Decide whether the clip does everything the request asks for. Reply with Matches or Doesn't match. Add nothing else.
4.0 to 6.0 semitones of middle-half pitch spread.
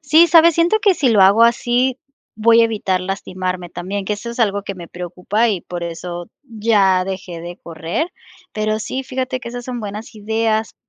Matches